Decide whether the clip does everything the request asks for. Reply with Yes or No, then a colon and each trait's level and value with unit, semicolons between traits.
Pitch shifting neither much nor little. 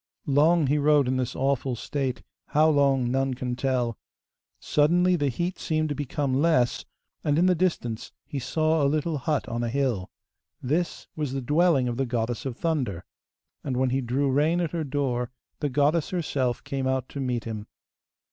Yes: average, 3.5 semitones